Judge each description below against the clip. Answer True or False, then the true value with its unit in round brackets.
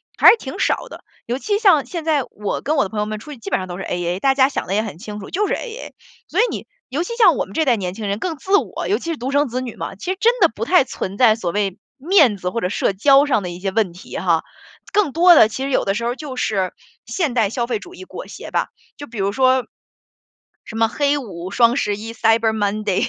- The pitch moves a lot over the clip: True (6.5 semitones)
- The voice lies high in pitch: True (235 Hz)